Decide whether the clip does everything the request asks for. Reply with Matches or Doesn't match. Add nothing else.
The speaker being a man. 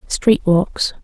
Doesn't match